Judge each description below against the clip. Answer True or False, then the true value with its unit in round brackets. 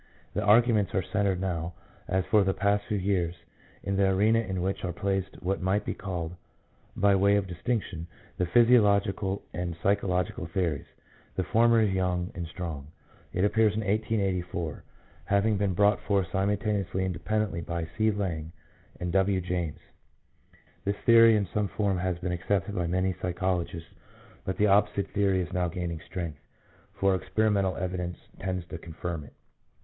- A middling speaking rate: True (165 wpm)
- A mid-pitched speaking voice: False (95 Hz)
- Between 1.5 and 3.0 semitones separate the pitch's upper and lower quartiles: True (2.5 semitones)